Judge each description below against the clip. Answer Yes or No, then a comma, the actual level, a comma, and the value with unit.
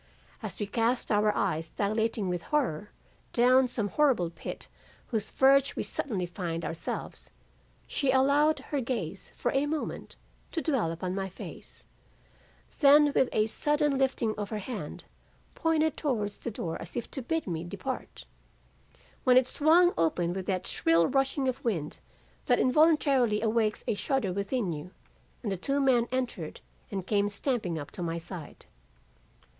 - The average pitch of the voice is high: Yes, high, 225 Hz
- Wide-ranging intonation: Yes, wide, 6.4 semitones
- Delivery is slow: No, average, 160 wpm